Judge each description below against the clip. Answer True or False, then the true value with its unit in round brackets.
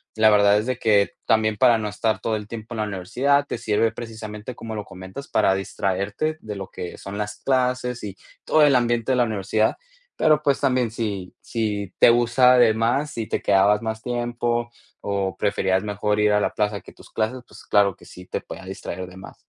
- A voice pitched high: False (110 Hz)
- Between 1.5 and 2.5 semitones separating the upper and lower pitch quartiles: False (2.9 semitones)